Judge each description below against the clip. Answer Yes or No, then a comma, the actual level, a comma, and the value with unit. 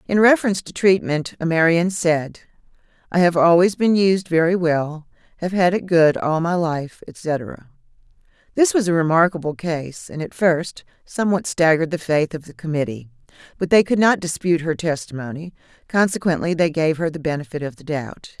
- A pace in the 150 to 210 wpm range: Yes, average, 170 wpm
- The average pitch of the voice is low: No, medium, 165 Hz